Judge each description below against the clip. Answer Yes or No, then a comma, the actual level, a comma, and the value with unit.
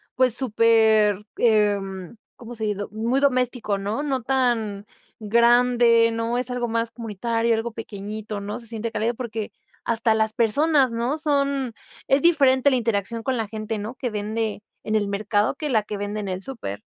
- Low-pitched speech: No, high, 230 Hz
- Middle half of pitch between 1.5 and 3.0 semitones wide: Yes, average, 2.7 semitones